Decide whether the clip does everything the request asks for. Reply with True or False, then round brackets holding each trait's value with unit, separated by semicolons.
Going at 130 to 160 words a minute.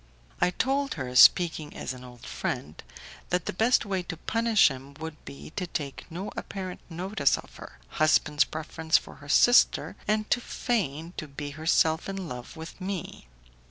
False (170 wpm)